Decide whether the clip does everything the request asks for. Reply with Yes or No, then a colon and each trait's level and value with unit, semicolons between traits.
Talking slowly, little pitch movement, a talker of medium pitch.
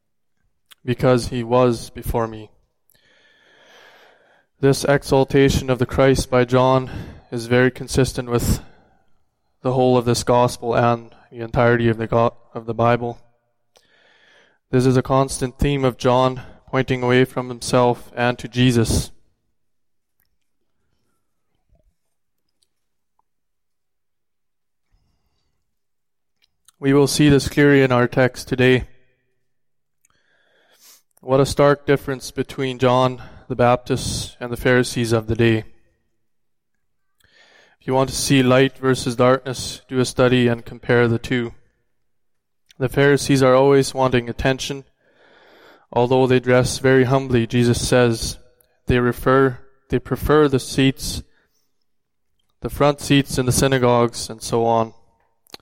No: slow, 120 wpm; narrow, 1.8 semitones; low, 125 Hz